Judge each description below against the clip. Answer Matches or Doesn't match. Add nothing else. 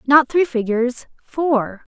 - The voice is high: Matches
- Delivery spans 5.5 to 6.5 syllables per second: Doesn't match